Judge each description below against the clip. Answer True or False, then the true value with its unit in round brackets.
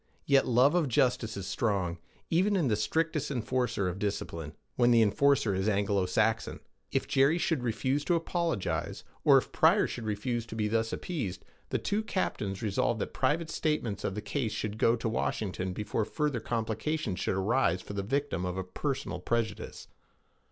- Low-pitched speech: True (115 Hz)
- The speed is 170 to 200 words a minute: True (175 wpm)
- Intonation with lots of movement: True (5.7 semitones)